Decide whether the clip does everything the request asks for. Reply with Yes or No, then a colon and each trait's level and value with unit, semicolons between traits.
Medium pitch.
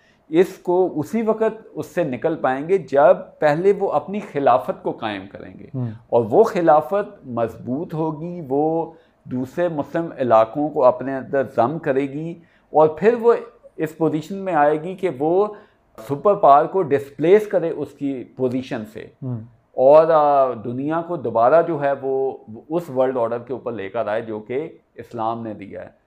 Yes: medium, 150 Hz